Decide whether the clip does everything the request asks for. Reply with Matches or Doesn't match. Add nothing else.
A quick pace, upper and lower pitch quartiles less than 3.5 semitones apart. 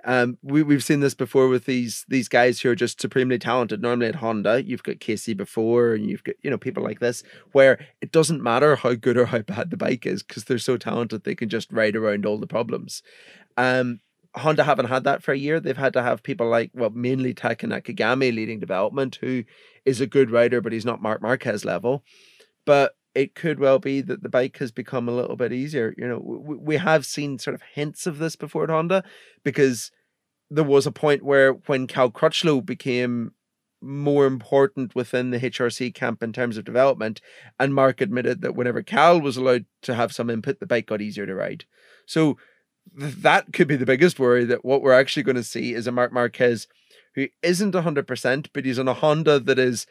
Matches